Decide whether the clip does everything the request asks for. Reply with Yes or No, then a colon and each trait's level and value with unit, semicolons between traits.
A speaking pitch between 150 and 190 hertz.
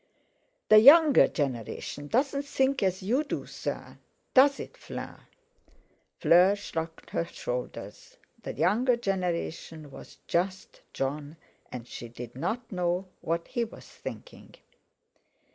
Yes: medium, 185 Hz